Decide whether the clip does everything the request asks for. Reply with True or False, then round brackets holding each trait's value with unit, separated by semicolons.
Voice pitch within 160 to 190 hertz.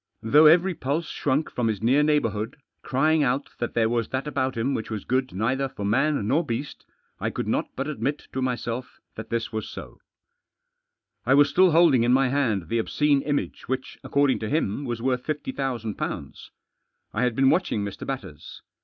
False (130 Hz)